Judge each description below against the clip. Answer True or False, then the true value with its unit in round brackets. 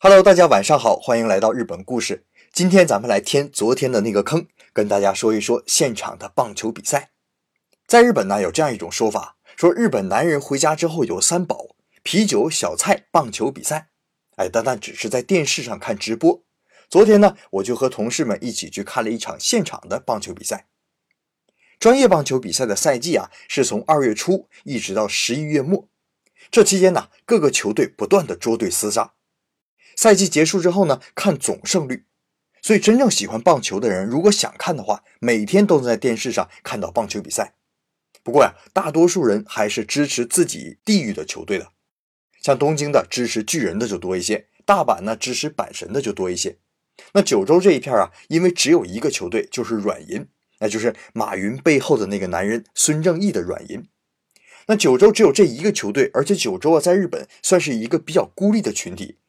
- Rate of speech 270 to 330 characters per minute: True (300 characters per minute)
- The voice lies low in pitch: False (175 Hz)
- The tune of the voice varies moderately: False (8.2 semitones)